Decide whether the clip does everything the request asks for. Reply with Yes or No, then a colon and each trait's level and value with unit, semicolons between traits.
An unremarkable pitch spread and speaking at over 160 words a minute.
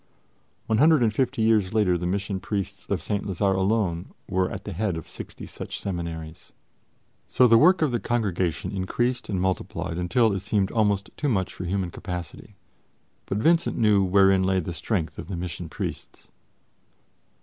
Yes: average, 3.6 semitones; average, 170 wpm